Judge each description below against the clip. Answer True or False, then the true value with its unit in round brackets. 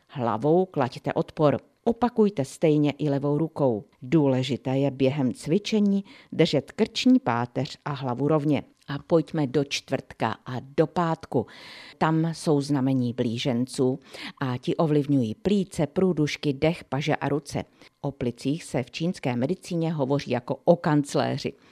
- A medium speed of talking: True (135 wpm)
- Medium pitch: True (145 Hz)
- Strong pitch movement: False (3.7 semitones)